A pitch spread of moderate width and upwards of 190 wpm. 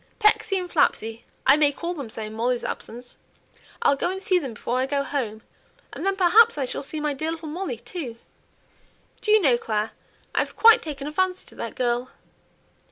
No: wide, 6.8 semitones; average, 200 wpm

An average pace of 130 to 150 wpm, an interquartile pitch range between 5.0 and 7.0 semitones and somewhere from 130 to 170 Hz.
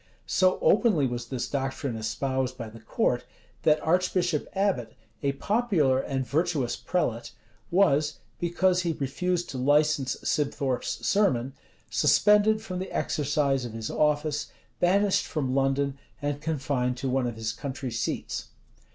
Yes: average, 140 wpm; average, 5.3 semitones; medium, 140 Hz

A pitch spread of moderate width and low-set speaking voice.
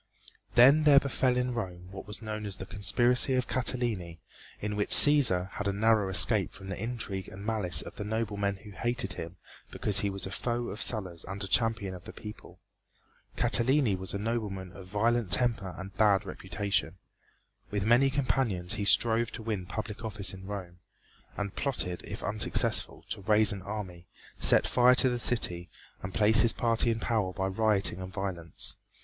Yes: average, 3.5 semitones; low, 105 Hz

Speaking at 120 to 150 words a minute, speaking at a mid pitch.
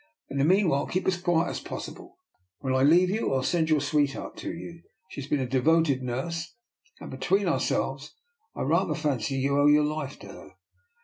No: average, 200 wpm; medium, 150 Hz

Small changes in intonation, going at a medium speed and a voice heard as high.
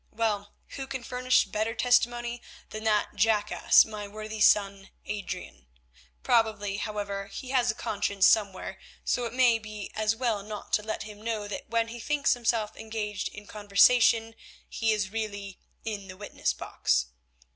Yes: narrow, 1.9 semitones; average, 155 wpm; high, 215 Hz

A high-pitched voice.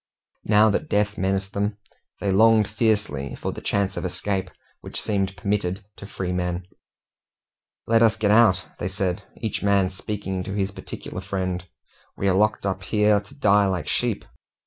No: low, 100 Hz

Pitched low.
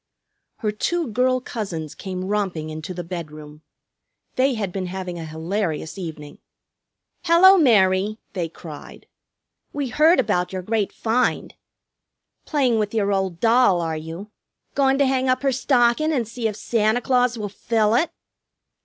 No: high, 210 Hz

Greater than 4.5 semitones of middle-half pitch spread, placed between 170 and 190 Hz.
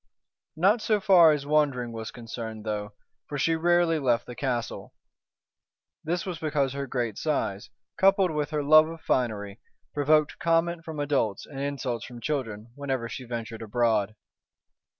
No: average, 5.3 semitones; medium, 140 Hz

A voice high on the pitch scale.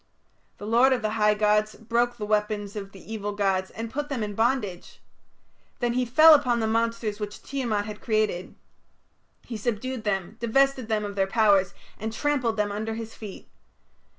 Yes: high, 220 Hz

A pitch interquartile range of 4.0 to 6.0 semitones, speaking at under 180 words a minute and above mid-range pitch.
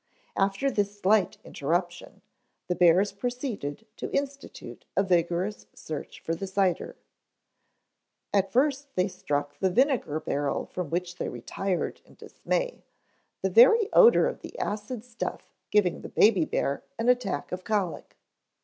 Yes: average, 5.1 semitones; average, 140 wpm; high, 195 Hz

